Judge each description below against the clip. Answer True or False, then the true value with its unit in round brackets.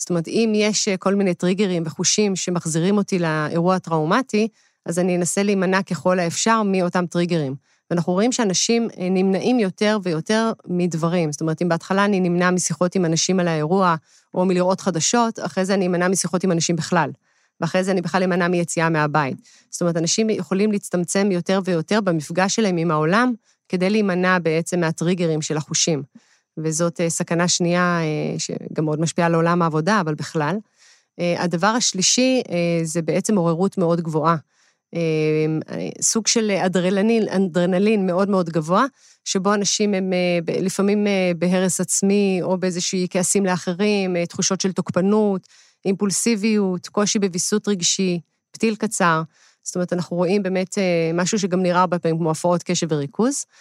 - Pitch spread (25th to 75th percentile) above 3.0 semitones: False (2.7 semitones)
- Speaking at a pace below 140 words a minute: False (145 wpm)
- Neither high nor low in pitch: True (180 Hz)